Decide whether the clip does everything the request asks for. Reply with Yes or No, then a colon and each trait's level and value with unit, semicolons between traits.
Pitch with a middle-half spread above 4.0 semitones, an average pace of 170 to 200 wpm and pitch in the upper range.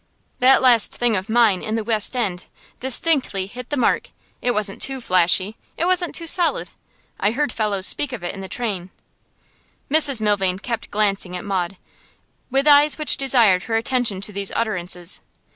Yes: average, 5.1 semitones; average, 175 wpm; high, 220 Hz